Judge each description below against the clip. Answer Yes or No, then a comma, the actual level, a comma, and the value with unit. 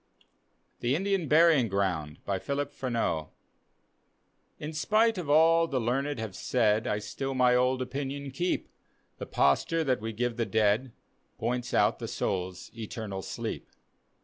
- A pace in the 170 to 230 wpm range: No, average, 140 wpm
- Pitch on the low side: Yes, low, 125 Hz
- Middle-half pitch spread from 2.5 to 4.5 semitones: No, wide, 5.4 semitones